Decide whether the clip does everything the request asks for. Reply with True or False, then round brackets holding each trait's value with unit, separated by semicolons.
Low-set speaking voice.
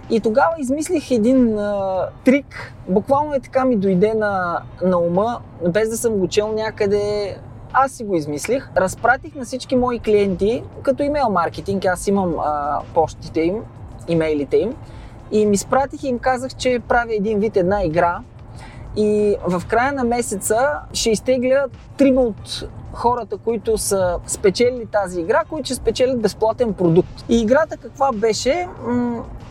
False (215 Hz)